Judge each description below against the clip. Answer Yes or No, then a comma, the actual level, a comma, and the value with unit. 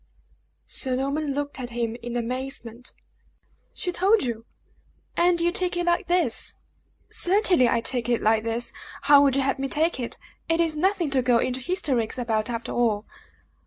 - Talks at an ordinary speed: Yes, average, 170 wpm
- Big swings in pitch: Yes, wide, 6.0 semitones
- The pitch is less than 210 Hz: No, very high, 265 Hz